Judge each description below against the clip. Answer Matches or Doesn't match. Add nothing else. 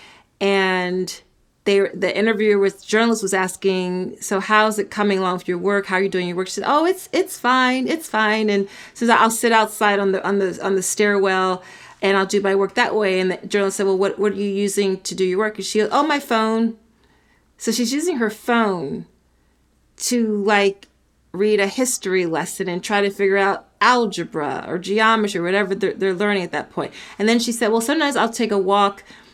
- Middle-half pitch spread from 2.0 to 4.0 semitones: Matches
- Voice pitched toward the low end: Doesn't match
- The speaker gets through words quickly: Matches